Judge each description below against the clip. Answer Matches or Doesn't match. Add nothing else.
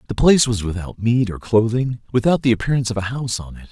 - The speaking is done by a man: Matches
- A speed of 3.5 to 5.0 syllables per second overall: Doesn't match